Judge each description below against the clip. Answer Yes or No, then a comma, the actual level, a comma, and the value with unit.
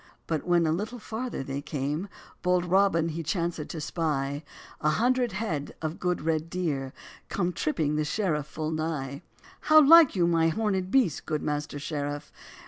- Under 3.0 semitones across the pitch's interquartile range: No, average, 3.9 semitones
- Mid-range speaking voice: Yes, medium, 165 Hz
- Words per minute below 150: No, average, 165 wpm